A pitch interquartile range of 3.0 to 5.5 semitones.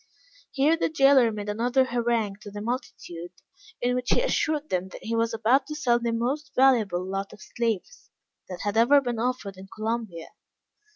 Yes: average, 4.1 semitones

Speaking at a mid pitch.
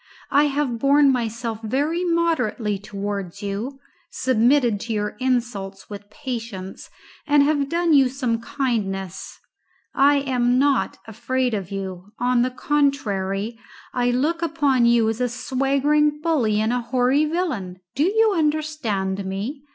No: very high, 250 Hz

